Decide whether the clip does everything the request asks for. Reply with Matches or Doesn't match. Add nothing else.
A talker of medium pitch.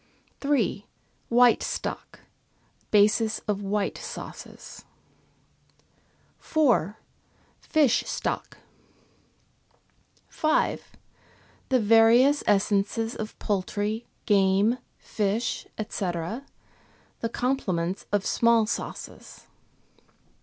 Doesn't match